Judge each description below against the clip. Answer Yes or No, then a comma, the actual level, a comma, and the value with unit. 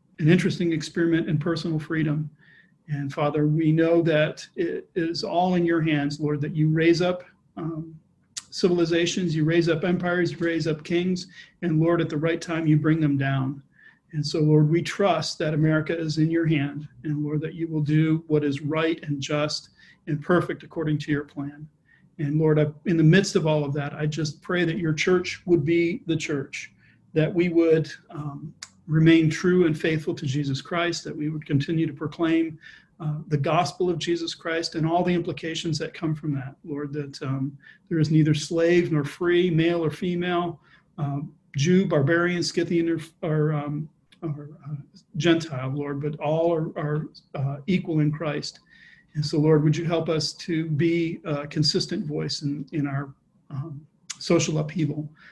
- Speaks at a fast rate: No, average, 185 wpm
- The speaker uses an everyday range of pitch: No, narrow, 2.1 semitones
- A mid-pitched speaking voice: Yes, medium, 160 Hz